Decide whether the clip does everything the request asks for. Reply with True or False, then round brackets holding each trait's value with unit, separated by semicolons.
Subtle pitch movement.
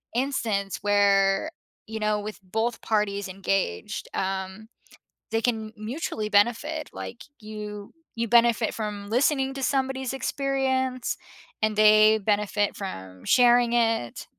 False (3.1 semitones)